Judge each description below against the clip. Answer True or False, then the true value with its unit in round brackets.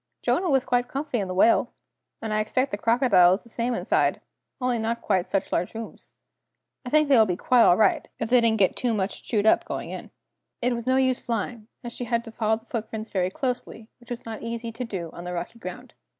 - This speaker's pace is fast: True (235 wpm)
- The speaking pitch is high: True (230 Hz)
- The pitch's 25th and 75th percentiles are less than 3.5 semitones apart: True (2.7 semitones)